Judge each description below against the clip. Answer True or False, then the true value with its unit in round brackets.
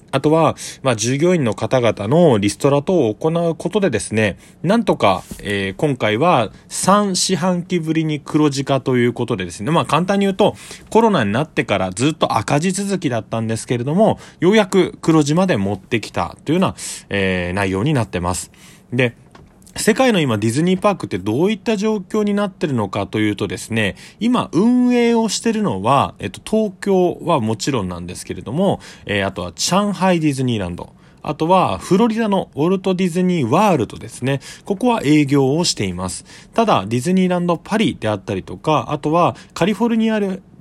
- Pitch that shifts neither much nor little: False (8.9 semitones)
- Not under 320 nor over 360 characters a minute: False (385 characters per minute)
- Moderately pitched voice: True (155 Hz)